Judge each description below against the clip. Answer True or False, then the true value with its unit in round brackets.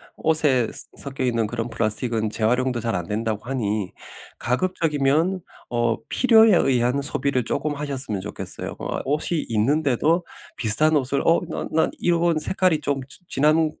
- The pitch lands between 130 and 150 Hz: True (135 Hz)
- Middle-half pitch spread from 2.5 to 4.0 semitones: False (5.1 semitones)